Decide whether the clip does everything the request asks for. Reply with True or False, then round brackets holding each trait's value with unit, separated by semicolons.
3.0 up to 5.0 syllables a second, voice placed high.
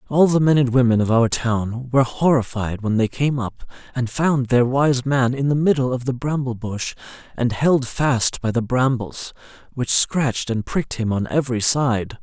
False (4.7 syllables/s; 125 Hz)